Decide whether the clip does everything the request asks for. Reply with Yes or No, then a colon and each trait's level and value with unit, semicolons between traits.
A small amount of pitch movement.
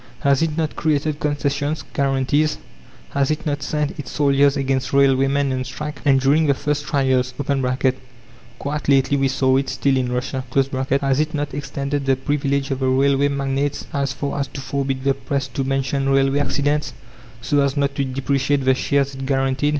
Yes: narrow, 1.2 semitones